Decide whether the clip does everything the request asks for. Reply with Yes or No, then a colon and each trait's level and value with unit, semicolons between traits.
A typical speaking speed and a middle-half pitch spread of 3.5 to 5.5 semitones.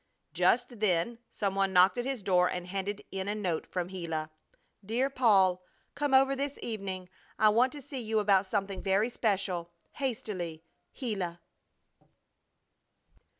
Yes: average, 145 wpm; average, 4.5 semitones